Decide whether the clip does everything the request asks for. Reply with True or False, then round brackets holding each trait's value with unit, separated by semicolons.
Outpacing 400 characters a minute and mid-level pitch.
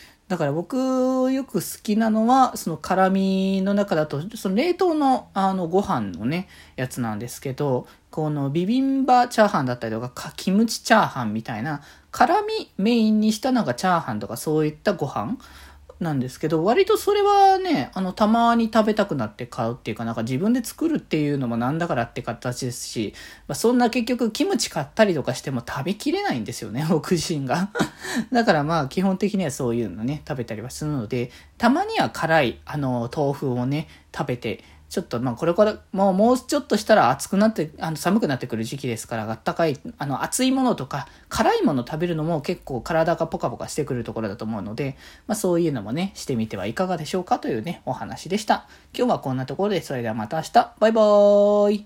True (415 characters per minute; 170 Hz)